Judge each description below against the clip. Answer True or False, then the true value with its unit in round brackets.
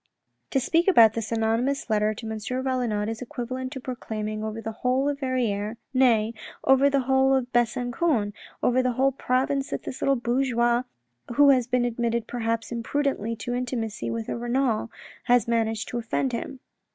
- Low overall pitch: False (240 Hz)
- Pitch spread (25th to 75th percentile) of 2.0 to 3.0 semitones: True (2.6 semitones)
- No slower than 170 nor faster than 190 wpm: True (175 wpm)